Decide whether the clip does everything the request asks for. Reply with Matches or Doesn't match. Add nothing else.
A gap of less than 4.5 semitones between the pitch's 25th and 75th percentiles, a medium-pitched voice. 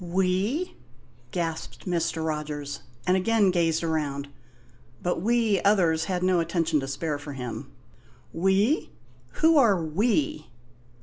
Matches